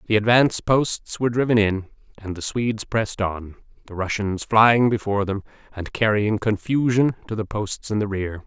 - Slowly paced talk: No, average, 175 wpm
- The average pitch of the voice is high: No, low, 105 Hz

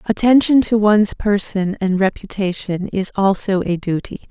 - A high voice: Yes, high, 200 Hz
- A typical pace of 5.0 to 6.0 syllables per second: No, 4.8 syllables/s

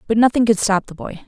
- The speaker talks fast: Yes, fast, 280 wpm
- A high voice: Yes, high, 210 Hz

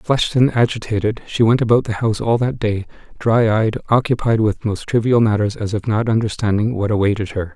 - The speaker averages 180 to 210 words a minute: Yes, average, 200 wpm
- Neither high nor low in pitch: No, low, 110 Hz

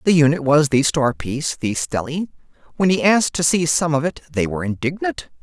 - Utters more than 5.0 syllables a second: Yes, 5.7 syllables/s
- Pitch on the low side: No, medium, 150 Hz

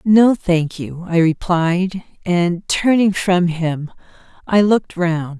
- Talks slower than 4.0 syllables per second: Yes, 3.3 syllables/s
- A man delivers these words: No, female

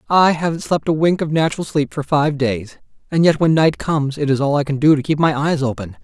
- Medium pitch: Yes, medium, 145 Hz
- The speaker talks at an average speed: No, fast, 270 wpm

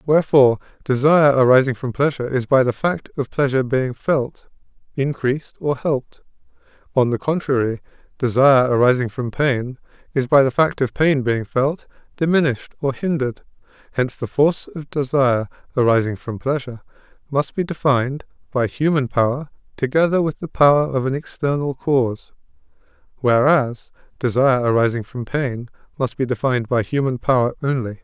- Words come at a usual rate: Yes, average, 145 wpm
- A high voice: No, low, 130 Hz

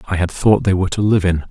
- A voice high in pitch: No, very low, 95 Hz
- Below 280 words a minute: No, fast, 320 wpm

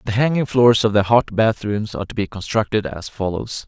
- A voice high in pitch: No, low, 105 Hz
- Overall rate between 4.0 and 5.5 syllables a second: Yes, 5.4 syllables/s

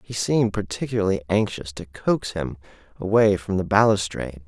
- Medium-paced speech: Yes, average, 150 wpm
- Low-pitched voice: Yes, very low, 95 Hz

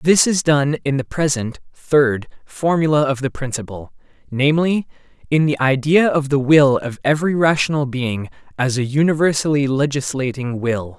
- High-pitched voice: No, medium, 140 Hz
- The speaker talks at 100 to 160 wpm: Yes, average, 150 wpm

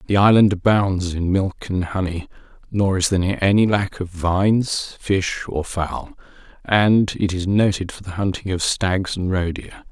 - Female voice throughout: No, male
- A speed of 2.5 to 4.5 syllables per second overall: Yes, 4.3 syllables/s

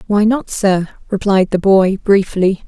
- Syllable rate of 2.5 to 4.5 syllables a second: Yes, 4.1 syllables/s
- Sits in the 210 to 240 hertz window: No, high, 195 Hz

